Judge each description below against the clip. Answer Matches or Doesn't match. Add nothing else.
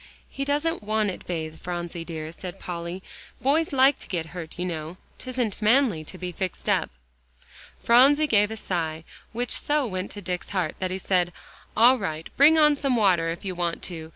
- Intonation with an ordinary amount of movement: Doesn't match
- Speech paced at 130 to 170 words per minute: Doesn't match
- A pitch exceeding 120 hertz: Matches